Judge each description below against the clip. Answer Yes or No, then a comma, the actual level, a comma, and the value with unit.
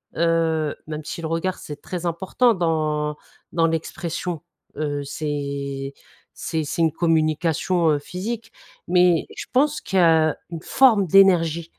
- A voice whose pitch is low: No, medium, 165 Hz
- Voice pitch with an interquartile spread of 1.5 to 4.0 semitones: Yes, average, 2.7 semitones